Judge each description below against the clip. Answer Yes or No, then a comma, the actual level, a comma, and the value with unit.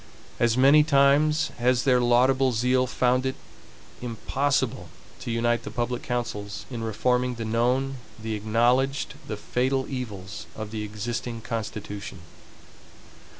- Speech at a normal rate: No, slow, 125 wpm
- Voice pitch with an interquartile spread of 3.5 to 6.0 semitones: No, average, 2.8 semitones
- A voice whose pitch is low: Yes, low, 120 Hz